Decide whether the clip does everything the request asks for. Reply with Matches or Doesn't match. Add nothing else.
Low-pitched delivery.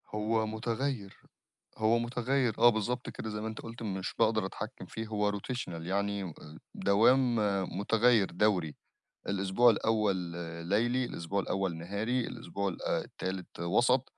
Matches